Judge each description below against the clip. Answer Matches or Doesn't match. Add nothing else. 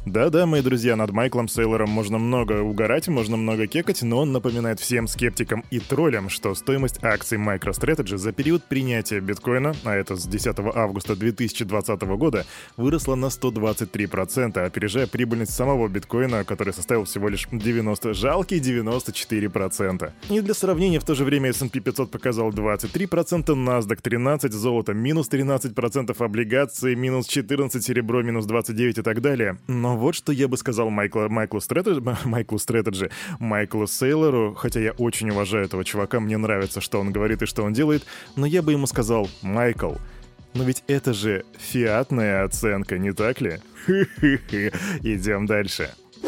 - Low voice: Matches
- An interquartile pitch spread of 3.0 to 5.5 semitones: Matches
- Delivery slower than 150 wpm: Doesn't match